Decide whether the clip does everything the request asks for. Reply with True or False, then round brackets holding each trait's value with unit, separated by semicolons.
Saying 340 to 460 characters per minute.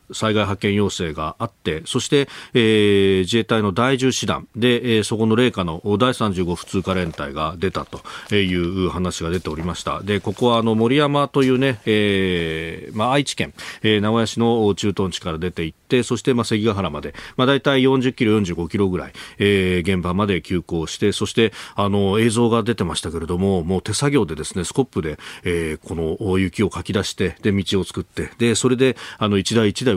True (360 characters per minute)